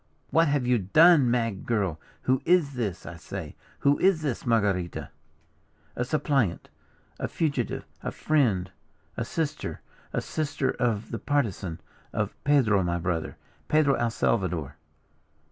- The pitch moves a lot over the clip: Yes, wide, 6.7 semitones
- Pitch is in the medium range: No, low, 120 Hz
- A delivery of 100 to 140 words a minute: Yes, slow, 135 wpm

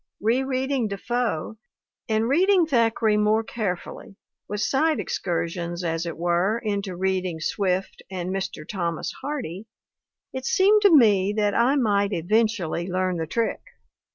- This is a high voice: Yes, high, 205 Hz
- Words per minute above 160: No, slow, 135 wpm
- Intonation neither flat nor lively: Yes, average, 4.7 semitones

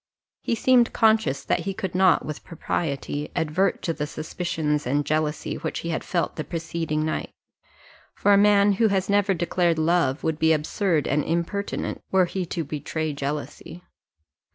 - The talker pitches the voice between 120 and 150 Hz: No, medium, 165 Hz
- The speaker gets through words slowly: No, average, 165 wpm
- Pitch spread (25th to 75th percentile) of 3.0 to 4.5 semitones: Yes, average, 3.8 semitones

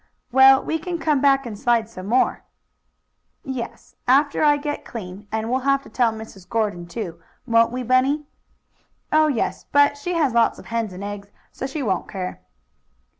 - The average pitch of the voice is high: Yes, high, 245 Hz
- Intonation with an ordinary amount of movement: Yes, average, 4.7 semitones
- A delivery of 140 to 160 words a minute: No, average, 175 wpm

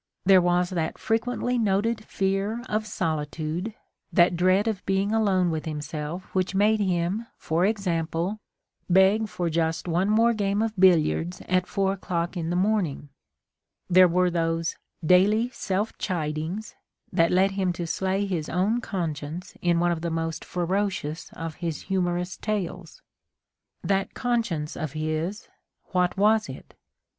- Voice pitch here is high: No, medium, 180 Hz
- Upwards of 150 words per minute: No, average, 140 wpm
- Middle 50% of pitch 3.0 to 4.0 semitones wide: Yes, average, 3.3 semitones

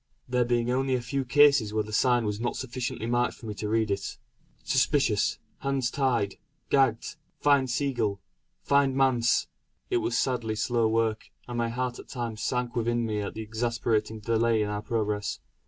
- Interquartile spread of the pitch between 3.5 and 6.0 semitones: No, average, 2.7 semitones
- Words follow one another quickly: No, average, 175 wpm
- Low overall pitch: Yes, low, 120 Hz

